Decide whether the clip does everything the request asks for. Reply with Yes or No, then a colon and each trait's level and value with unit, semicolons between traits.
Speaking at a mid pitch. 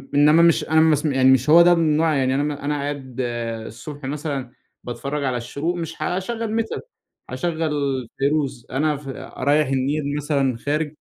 Yes: medium, 145 Hz